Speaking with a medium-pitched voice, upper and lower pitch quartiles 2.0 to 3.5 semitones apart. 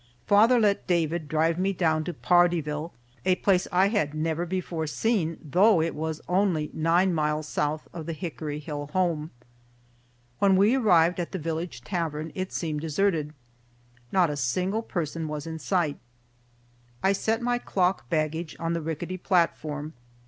Yes: medium, 165 Hz; average, 3.2 semitones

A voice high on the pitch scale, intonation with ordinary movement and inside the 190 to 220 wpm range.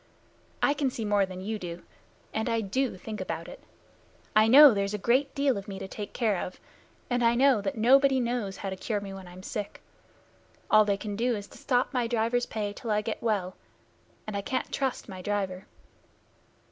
Yes: high, 215 Hz; average, 3.6 semitones; fast, 205 wpm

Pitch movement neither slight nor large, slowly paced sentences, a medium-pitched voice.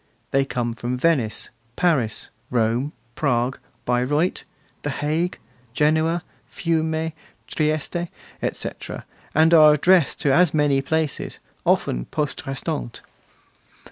Yes: average, 4.2 semitones; slow, 105 wpm; medium, 150 Hz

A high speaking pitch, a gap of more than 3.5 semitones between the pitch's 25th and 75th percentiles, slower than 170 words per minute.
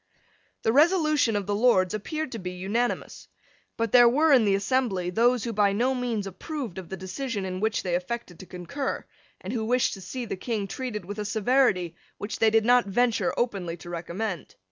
No: high, 220 Hz; average, 4.6 semitones; average, 200 wpm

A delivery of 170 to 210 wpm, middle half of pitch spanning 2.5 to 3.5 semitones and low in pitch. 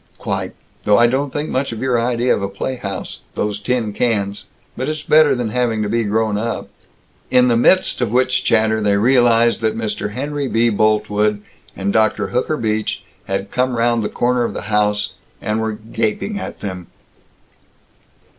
Yes: average, 175 wpm; average, 3.0 semitones; low, 115 Hz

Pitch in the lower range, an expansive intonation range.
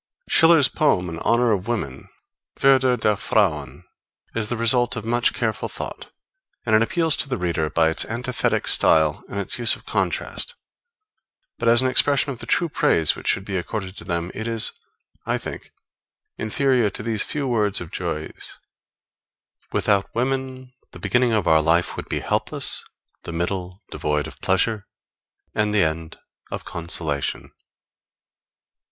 Yes: low, 110 Hz; wide, 6.0 semitones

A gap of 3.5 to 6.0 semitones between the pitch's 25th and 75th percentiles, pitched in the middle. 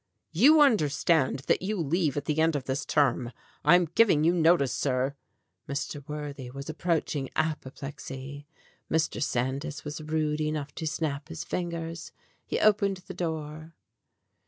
No: average, 2.9 semitones; medium, 155 Hz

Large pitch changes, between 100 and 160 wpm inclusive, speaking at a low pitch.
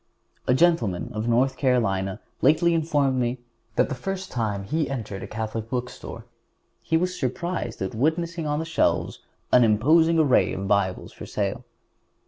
Yes: wide, 6.8 semitones; average, 155 wpm; low, 130 Hz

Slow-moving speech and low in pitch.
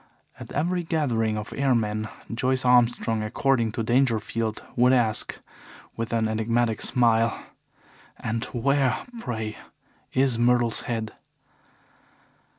Yes: slow, 105 wpm; low, 115 Hz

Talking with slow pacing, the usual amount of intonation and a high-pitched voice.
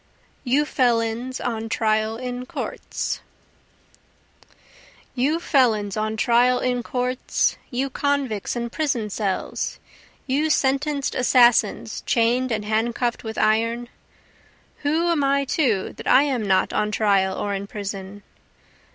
Yes: slow, 120 wpm; average, 3.4 semitones; high, 240 Hz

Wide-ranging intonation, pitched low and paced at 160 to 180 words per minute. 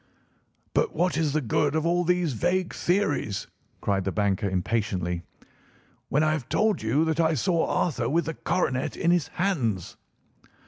No: wide, 7.9 semitones; medium, 155 Hz; average, 165 wpm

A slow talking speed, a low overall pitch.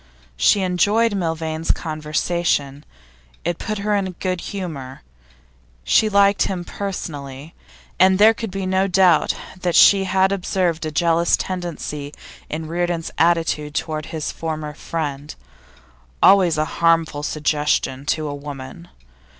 No: slow, 130 wpm; medium, 165 Hz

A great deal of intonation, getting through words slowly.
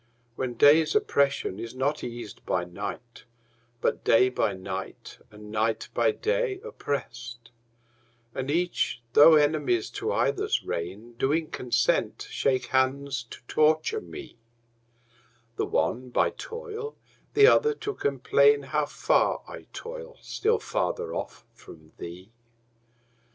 Yes: wide, 7.2 semitones; slow, 125 wpm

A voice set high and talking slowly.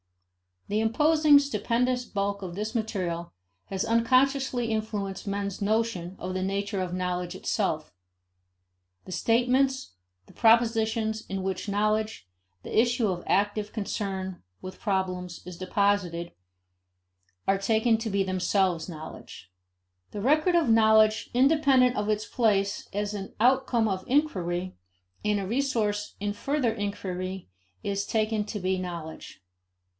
Yes: high, 205 Hz; slow, 130 wpm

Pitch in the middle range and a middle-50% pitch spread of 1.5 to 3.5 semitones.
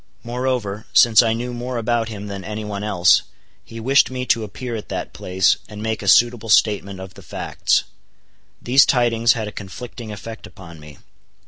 No: low, 110 Hz; average, 2.9 semitones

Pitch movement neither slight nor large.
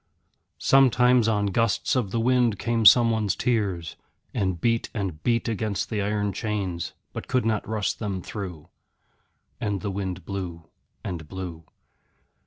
Yes: average, 3.5 semitones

